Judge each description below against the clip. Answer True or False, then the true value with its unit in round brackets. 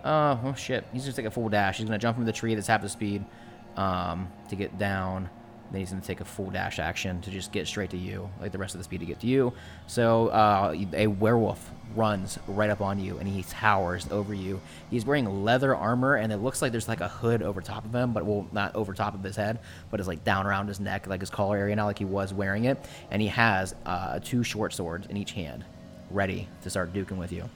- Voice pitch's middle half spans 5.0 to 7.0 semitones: False (3.2 semitones)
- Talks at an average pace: False (265 wpm)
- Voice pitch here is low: True (100 Hz)